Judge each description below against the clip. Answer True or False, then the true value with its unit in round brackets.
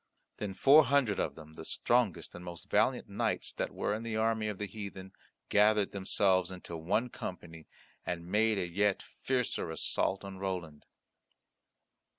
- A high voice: False (100 Hz)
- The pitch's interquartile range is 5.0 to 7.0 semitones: False (3.5 semitones)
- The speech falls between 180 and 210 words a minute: False (160 wpm)